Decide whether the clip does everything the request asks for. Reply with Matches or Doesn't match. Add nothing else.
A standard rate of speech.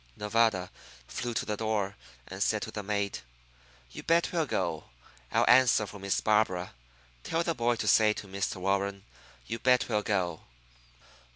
Matches